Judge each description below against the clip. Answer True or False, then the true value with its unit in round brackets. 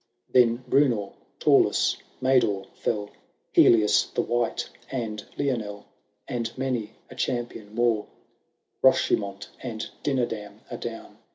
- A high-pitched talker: False (115 Hz)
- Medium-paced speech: False (105 wpm)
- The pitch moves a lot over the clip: False (3.1 semitones)